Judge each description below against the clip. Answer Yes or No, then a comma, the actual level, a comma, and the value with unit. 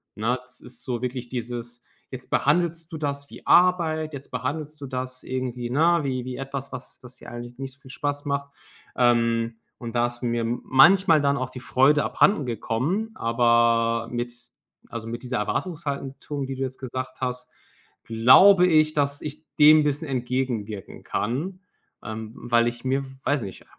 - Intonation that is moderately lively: Yes, average, 3.4 semitones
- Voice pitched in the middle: No, low, 130 Hz